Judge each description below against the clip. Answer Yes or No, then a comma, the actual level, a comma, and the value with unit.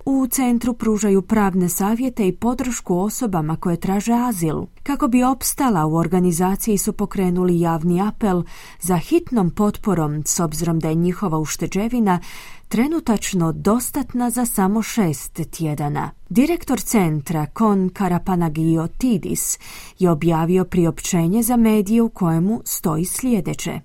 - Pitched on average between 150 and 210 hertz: Yes, high, 190 Hz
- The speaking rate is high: No, average, 125 wpm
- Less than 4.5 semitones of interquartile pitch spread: No, average, 5.2 semitones